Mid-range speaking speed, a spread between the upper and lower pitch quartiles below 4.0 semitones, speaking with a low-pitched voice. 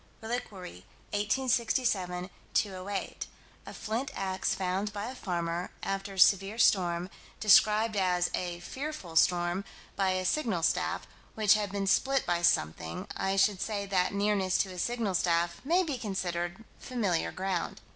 No: average, 145 wpm; average, 3.2 semitones; high, 195 Hz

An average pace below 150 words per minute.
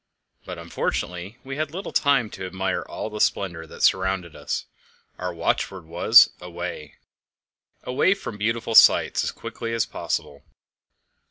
Yes: average, 140 wpm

